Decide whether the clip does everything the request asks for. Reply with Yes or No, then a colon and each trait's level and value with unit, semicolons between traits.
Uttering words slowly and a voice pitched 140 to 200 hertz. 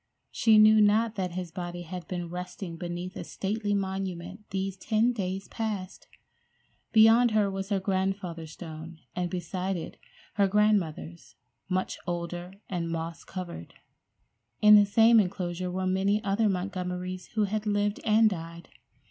No: average, 145 wpm; high, 190 Hz